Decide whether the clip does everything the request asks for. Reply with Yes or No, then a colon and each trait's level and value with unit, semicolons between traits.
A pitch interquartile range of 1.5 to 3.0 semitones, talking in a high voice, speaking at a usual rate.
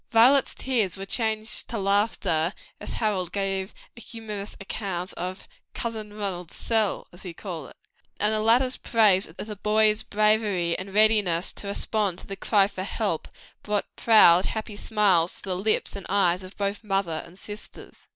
Yes: narrow, 2.6 semitones; high, 205 Hz; average, 170 wpm